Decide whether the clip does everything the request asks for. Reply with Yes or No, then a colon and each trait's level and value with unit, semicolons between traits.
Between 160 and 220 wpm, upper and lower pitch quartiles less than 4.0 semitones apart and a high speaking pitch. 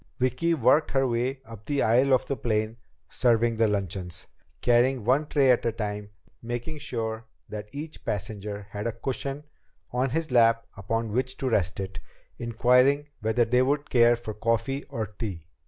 No: average, 170 wpm; average, 3.3 semitones; low, 120 Hz